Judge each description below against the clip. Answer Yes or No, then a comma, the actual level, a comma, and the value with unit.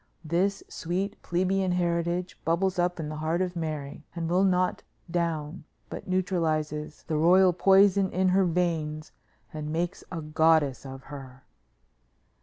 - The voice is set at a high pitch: No, medium, 170 Hz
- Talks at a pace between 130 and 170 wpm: Yes, average, 140 wpm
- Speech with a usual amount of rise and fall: Yes, average, 3.0 semitones